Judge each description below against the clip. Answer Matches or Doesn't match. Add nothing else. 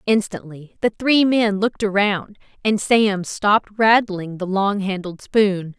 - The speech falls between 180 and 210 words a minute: Doesn't match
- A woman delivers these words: Matches